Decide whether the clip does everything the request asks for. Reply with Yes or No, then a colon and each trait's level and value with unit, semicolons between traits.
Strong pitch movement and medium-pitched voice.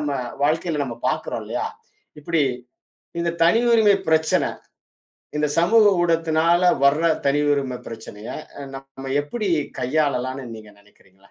No: average, 4.4 semitones; medium, 150 Hz